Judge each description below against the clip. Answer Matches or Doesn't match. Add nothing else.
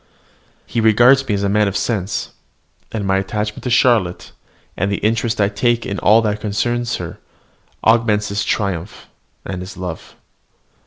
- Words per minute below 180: Matches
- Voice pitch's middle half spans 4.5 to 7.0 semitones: Doesn't match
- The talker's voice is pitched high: Doesn't match